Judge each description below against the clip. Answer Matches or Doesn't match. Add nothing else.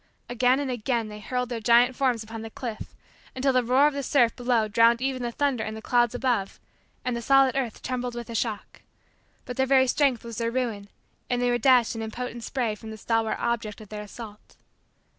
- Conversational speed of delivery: Doesn't match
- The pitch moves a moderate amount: Doesn't match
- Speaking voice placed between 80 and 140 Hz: Doesn't match